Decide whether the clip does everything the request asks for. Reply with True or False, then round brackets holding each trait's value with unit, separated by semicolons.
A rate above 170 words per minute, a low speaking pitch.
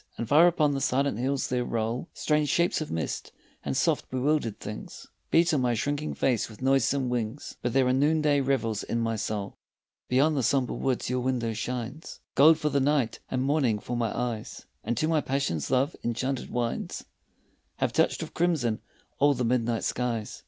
True (185 wpm; 130 Hz)